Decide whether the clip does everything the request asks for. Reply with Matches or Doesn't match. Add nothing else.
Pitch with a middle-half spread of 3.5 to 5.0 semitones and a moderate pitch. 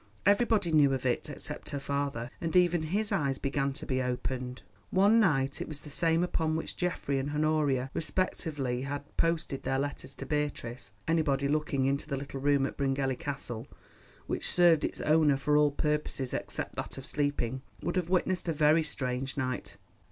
Doesn't match